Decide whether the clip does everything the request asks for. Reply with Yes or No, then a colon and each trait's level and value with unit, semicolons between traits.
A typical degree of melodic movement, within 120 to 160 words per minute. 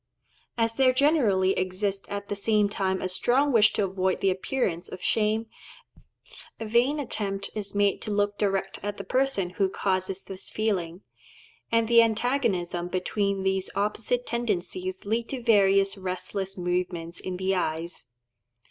Yes: average, 3.1 semitones; average, 150 wpm